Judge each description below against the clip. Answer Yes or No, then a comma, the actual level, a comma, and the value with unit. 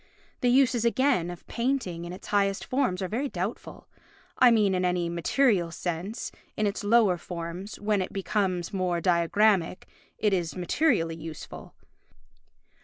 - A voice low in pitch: No, high, 190 Hz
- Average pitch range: Yes, average, 4.6 semitones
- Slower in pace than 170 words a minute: Yes, average, 140 wpm